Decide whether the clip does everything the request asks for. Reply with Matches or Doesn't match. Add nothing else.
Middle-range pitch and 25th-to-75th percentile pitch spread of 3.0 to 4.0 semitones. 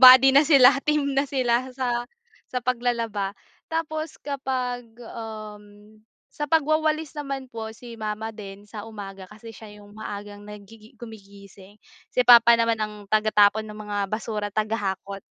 Doesn't match